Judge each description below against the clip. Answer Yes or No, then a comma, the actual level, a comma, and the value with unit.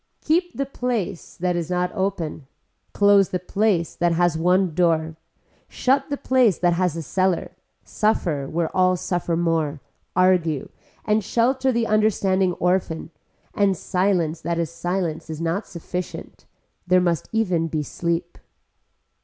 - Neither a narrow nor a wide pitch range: Yes, average, 3.2 semitones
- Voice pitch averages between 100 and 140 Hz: No, medium, 180 Hz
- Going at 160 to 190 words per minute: No, average, 140 wpm